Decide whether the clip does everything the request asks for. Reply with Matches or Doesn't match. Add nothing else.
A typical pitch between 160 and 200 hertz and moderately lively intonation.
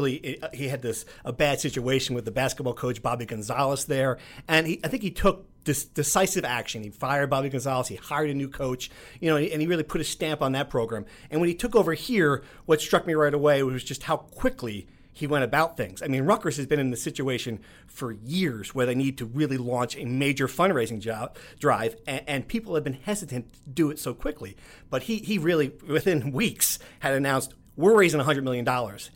Doesn't match